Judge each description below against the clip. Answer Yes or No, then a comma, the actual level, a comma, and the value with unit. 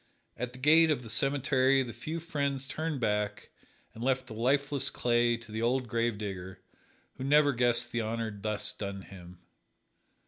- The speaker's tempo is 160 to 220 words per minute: Yes, average, 165 wpm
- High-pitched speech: No, low, 120 Hz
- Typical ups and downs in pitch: Yes, average, 3.9 semitones